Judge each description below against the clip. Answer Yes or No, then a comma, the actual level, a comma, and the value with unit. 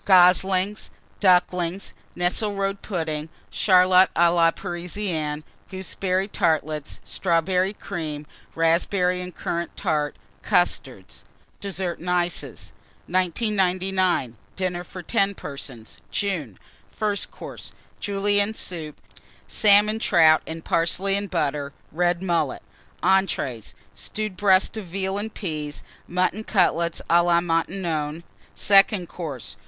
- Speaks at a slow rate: Yes, slow, 105 wpm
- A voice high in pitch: No, medium, 180 Hz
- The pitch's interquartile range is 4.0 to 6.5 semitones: No, average, 2.9 semitones